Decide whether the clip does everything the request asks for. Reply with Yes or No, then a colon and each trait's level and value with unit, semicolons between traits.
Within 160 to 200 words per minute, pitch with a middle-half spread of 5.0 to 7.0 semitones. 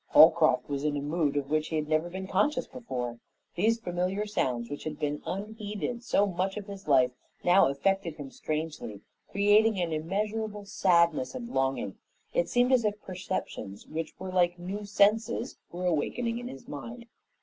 Yes: average, 170 wpm; wide, 5.6 semitones